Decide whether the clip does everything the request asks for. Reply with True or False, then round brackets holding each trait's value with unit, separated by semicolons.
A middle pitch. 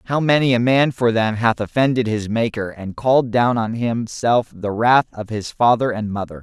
False (115 Hz)